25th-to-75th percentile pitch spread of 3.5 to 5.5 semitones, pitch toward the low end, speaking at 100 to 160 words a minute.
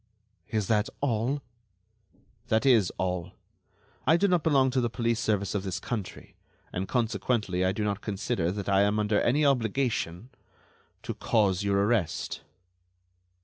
Yes: average, 4.0 semitones; low, 110 Hz; average, 145 wpm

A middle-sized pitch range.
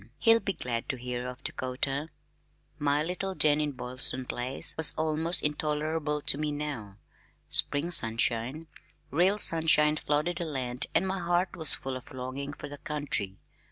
Yes: average, 3.9 semitones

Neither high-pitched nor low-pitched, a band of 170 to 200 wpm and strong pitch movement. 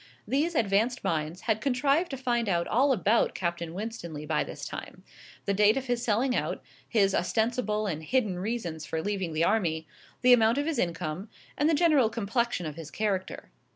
No: high, 215 Hz; average, 185 wpm; wide, 6.2 semitones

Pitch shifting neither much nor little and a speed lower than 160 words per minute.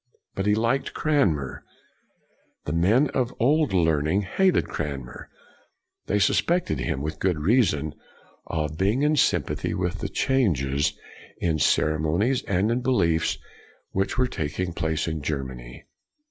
No: wide, 7.9 semitones; average, 145 wpm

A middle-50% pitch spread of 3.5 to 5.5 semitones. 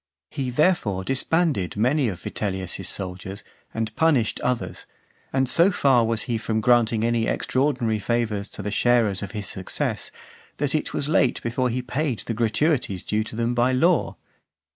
Yes: average, 3.9 semitones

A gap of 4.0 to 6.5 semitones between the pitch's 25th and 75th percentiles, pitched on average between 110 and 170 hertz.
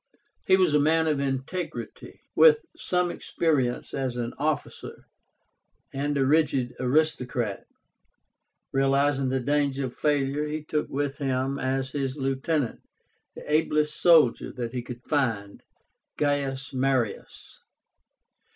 No: narrow, 2.4 semitones; medium, 140 Hz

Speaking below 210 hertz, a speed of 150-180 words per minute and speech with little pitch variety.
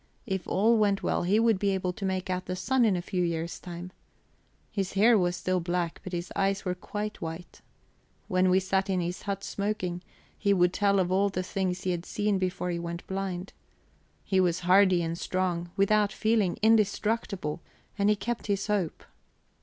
No: high, 190 Hz; average, 195 wpm; narrow, 2.2 semitones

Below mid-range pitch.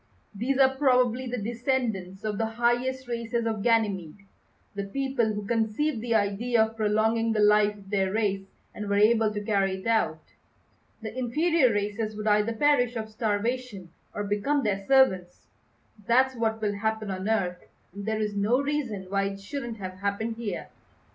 No: high, 220 Hz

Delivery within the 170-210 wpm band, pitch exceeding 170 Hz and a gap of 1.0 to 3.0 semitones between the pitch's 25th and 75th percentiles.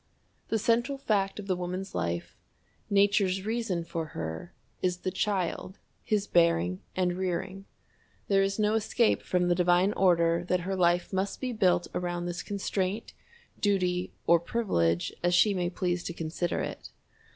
No: average, 155 wpm; medium, 185 Hz; narrow, 2.4 semitones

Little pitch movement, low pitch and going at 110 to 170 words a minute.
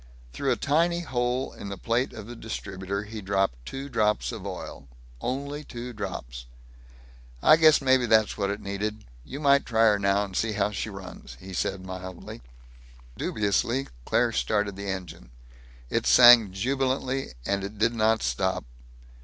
No: average, 4.3 semitones; low, 105 Hz; average, 160 wpm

